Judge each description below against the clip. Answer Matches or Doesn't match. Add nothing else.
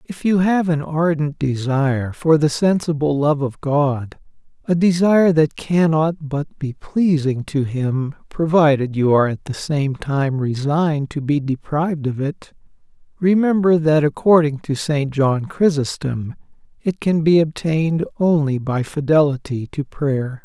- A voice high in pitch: Doesn't match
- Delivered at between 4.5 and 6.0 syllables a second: Doesn't match